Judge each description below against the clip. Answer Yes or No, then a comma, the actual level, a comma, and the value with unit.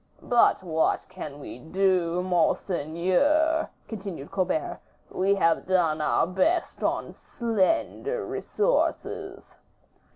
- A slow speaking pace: Yes, slow, 95 wpm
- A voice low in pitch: No, medium, 185 Hz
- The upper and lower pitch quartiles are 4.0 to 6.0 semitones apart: Yes, wide, 5.4 semitones